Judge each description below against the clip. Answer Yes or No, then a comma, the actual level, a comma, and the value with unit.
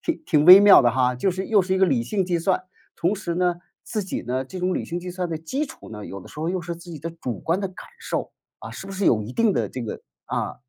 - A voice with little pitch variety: No, average, 4.6 semitones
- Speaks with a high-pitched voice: No, medium, 175 Hz